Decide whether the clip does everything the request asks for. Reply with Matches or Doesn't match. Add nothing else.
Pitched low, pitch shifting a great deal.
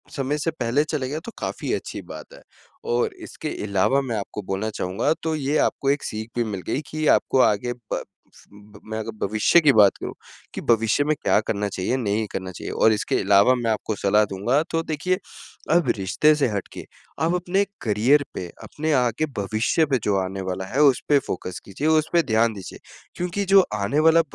Matches